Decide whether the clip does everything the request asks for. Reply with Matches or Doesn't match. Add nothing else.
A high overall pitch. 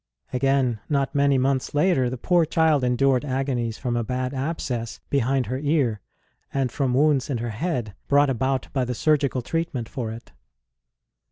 Doesn't match